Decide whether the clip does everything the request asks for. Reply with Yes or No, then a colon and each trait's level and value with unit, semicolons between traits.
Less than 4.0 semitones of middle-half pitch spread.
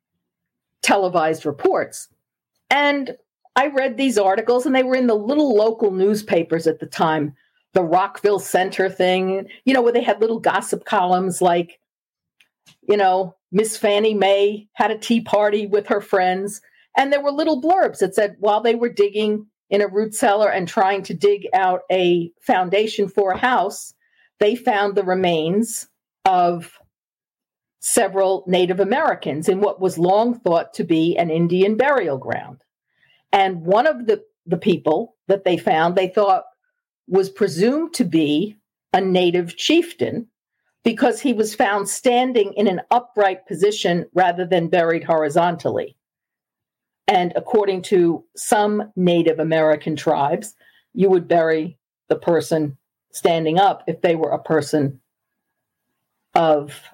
No: average, 4.6 semitones